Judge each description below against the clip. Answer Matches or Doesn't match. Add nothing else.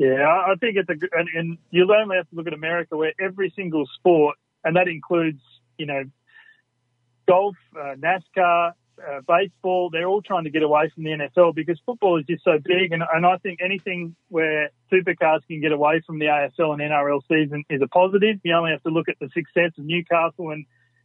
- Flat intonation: Doesn't match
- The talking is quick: Matches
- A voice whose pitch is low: Doesn't match